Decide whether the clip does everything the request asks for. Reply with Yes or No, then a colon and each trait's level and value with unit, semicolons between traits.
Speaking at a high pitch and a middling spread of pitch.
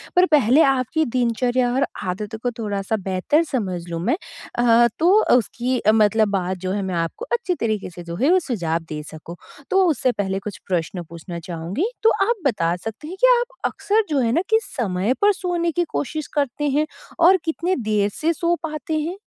No: high, 240 Hz; wide, 9.0 semitones